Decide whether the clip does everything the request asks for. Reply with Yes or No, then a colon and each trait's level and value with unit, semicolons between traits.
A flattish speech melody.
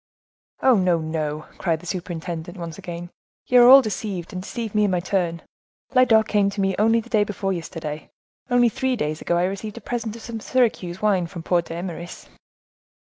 No: average, 4.3 semitones